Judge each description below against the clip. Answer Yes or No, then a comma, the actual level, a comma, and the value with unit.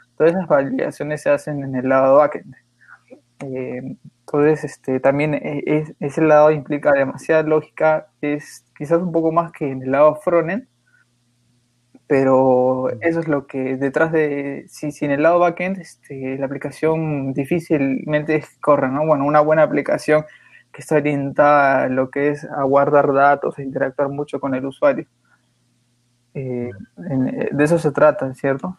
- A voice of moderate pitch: Yes, medium, 145 Hz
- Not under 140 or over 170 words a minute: Yes, average, 150 wpm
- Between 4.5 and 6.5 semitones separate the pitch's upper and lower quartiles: No, narrow, 2.4 semitones